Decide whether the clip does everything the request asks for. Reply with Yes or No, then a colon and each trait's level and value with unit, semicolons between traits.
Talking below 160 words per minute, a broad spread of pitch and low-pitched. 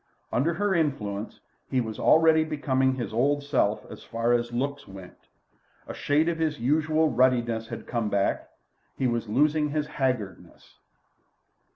No: average, 150 wpm; average, 4.6 semitones; low, 130 Hz